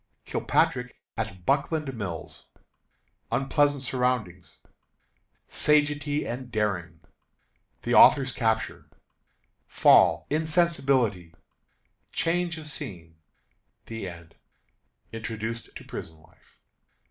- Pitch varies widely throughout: Yes, wide, 7.4 semitones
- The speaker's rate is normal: No, slow, 80 wpm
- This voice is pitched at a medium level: No, low, 125 Hz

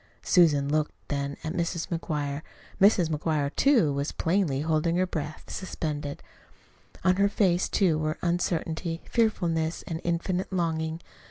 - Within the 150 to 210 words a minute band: No, slow, 135 wpm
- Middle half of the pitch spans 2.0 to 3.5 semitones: Yes, average, 2.8 semitones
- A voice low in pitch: No, medium, 165 Hz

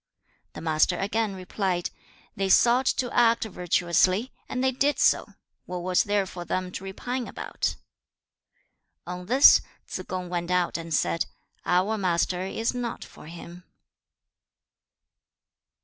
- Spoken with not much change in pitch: No, average, 4.2 semitones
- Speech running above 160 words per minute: No, slow, 135 wpm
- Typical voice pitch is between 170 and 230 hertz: Yes, medium, 185 Hz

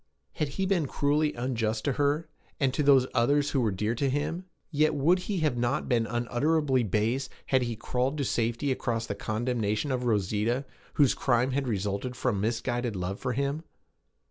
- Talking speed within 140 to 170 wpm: No, average, 180 wpm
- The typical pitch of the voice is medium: No, low, 125 Hz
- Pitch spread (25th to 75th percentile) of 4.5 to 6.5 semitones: No, average, 3.8 semitones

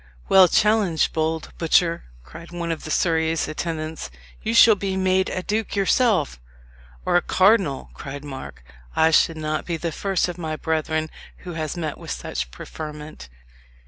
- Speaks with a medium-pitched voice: Yes, medium, 160 Hz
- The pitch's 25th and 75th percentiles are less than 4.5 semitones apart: Yes, average, 3.0 semitones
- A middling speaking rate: Yes, average, 155 wpm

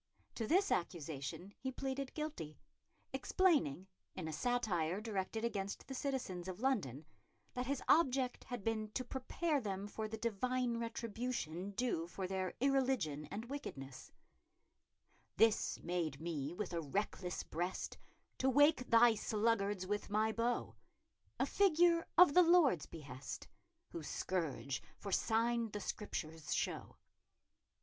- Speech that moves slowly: Yes, slow, 130 wpm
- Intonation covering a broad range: Yes, wide, 6.3 semitones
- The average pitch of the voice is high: Yes, high, 215 Hz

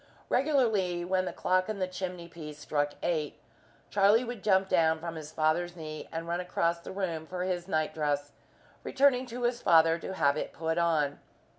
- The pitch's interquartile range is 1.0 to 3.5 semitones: Yes, average, 3.0 semitones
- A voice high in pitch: No, medium, 175 Hz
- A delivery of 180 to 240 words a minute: Yes, average, 185 wpm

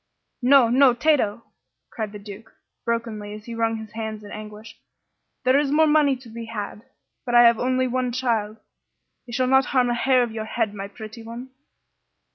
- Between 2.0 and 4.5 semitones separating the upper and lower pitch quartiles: Yes, average, 2.9 semitones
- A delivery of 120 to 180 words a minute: No, average, 190 wpm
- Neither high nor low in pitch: No, high, 235 Hz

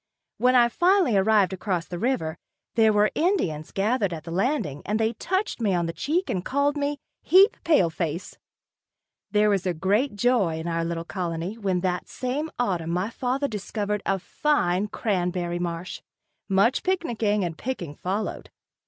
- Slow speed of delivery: No, average, 160 wpm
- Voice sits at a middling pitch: No, high, 205 Hz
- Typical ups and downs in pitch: No, wide, 6.2 semitones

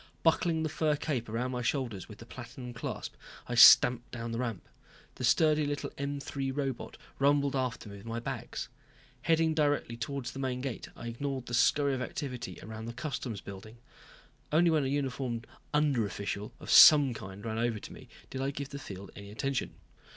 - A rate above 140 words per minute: Yes, average, 190 wpm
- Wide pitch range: No, average, 3.6 semitones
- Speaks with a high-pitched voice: No, low, 125 Hz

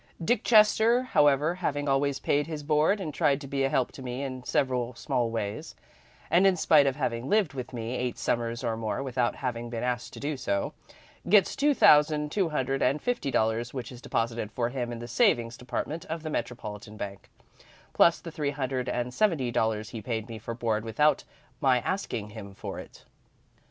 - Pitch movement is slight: No, average, 4.2 semitones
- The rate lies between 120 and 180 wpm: No, average, 195 wpm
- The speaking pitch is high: No, low, 130 Hz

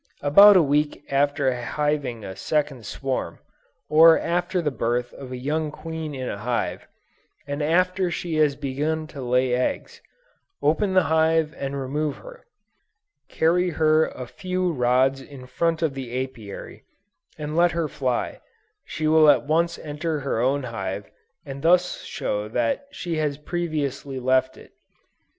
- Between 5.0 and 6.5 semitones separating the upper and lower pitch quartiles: No, average, 3.8 semitones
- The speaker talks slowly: No, average, 150 wpm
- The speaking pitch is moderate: Yes, medium, 145 Hz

